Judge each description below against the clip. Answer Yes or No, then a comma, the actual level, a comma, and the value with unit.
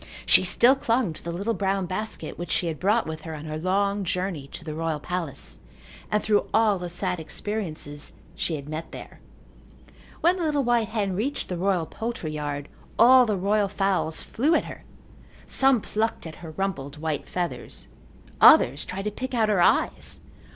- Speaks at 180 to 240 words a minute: Yes, average, 185 wpm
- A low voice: No, high, 190 Hz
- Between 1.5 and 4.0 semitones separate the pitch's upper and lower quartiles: No, average, 5.2 semitones